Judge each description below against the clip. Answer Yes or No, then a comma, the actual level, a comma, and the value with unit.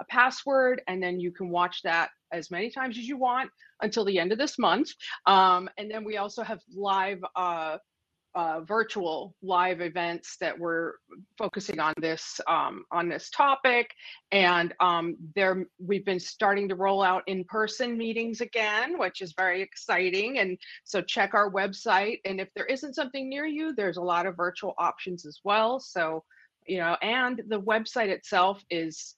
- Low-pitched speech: No, high, 195 Hz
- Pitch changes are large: No, average, 4.1 semitones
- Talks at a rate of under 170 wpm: No, average, 175 wpm